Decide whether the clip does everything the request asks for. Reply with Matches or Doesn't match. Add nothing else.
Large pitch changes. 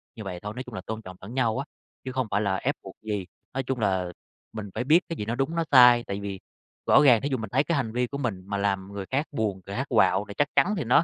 Doesn't match